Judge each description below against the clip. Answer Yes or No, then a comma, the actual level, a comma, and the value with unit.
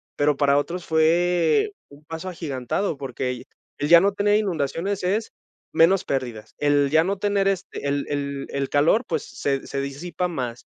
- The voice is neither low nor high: Yes, medium, 160 Hz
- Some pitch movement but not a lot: Yes, average, 4.7 semitones